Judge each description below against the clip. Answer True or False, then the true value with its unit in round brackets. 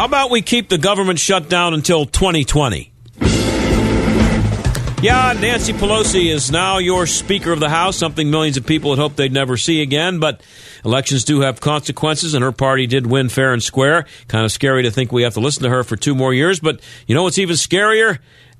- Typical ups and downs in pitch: False (5.8 semitones)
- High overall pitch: False (150 Hz)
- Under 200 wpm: False (205 wpm)